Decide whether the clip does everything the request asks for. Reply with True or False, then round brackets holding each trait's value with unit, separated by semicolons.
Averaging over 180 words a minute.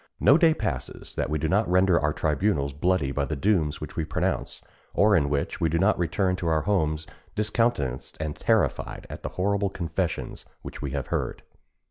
True (190 wpm)